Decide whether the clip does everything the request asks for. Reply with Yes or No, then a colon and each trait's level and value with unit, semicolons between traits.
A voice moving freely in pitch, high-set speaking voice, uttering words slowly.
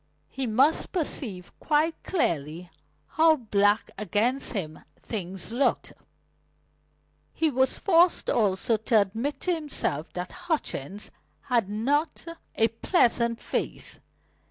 Yes: wide, 6.8 semitones; high, 230 Hz; slow, 110 wpm